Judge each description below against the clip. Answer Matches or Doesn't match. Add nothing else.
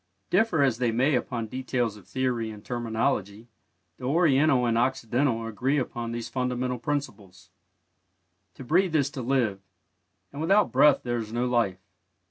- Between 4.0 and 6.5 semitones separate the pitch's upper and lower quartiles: Doesn't match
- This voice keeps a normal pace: Matches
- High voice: Doesn't match